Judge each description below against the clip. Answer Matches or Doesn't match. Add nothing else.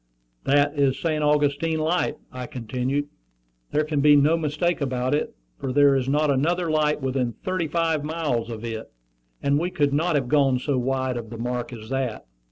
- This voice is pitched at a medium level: Matches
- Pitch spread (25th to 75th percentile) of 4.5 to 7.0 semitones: Doesn't match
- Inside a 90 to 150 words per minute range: Doesn't match